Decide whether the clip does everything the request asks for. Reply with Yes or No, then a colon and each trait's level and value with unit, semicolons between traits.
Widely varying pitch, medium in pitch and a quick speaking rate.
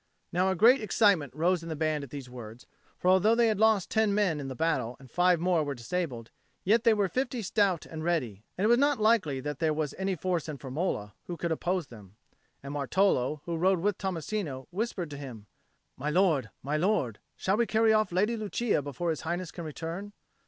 Yes: wide, 5.9 semitones; medium, 170 Hz; fast, 215 wpm